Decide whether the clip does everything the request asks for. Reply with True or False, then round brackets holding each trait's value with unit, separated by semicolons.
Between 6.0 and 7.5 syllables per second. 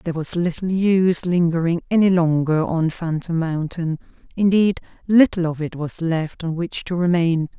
False (4.8 syllables/s)